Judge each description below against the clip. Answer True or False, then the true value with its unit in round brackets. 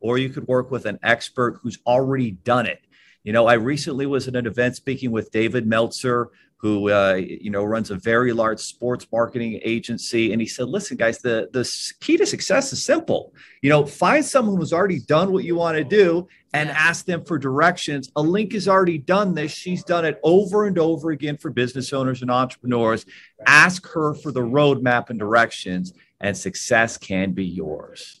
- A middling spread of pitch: False (6.1 semitones)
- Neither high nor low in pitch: False (130 Hz)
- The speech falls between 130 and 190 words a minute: False (200 wpm)